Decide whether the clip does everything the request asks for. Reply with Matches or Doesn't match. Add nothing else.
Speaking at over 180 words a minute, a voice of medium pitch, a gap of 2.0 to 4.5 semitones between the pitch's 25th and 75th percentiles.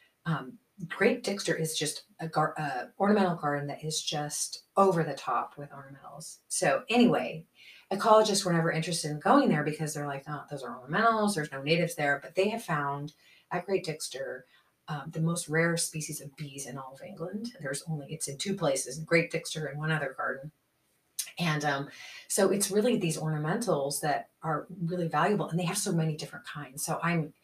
Matches